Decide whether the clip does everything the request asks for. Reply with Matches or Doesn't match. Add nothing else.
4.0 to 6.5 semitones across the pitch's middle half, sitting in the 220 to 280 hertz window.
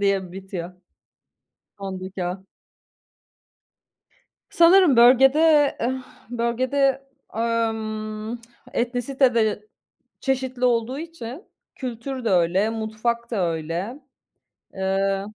Matches